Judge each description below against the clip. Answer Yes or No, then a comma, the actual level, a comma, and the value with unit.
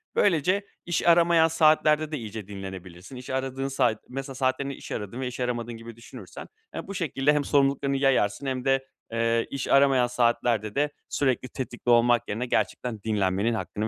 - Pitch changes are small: No, average, 3.3 semitones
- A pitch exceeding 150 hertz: No, low, 125 Hz